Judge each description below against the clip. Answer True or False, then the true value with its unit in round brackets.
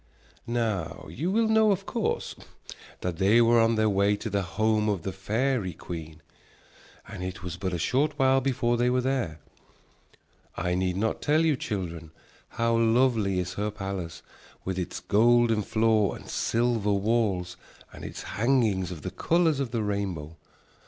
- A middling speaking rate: True (165 wpm)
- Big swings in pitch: False (4.5 semitones)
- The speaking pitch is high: False (110 Hz)